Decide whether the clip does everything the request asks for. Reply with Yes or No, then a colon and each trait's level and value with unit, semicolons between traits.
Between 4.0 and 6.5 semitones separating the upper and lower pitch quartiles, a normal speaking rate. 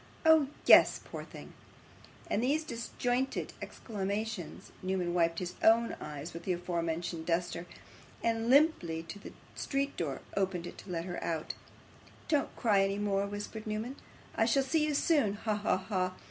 Yes: average, 5.1 semitones; average, 160 wpm